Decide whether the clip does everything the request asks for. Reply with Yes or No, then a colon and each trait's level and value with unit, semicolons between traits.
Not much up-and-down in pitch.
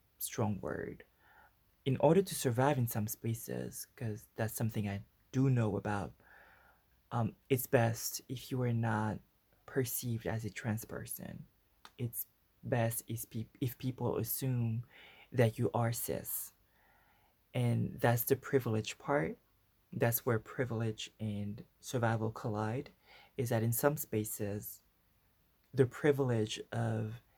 No: average, 3.0 semitones